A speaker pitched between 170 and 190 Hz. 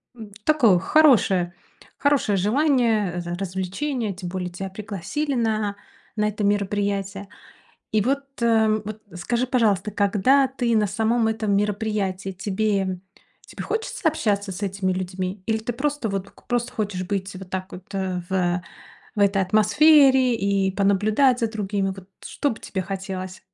No: high, 205 Hz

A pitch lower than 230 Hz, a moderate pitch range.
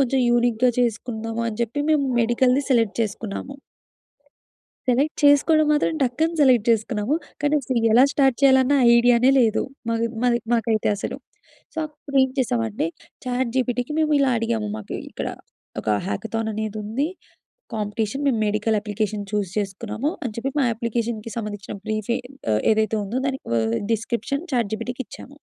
No: high, 235 Hz; average, 3.4 semitones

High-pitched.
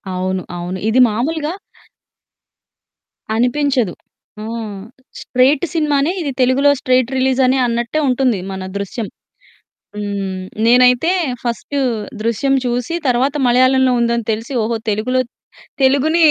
Yes: very high, 250 Hz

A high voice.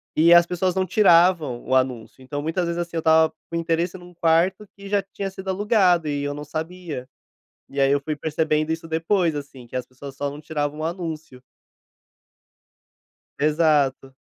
No: medium, 160 Hz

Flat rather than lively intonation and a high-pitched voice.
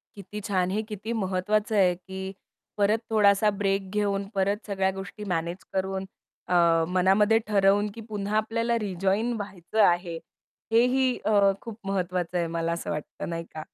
Yes: narrow, 2.3 semitones; high, 195 Hz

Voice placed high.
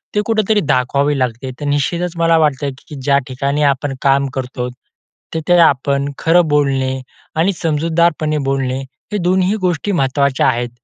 No: medium, 145 Hz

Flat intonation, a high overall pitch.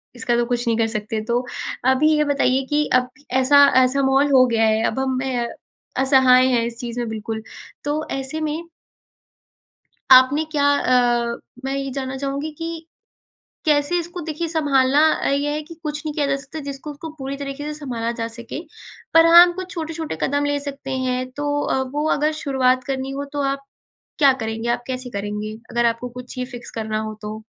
No: average, 3.2 semitones; very high, 270 Hz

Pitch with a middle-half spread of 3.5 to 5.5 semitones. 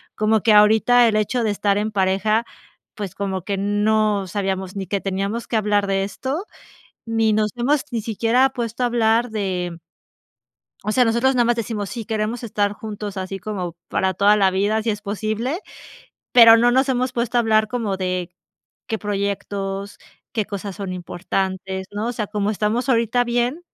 No: average, 2.8 semitones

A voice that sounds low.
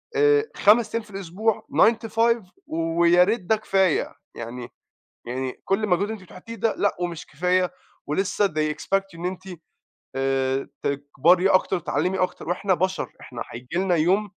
No: medium, 185 Hz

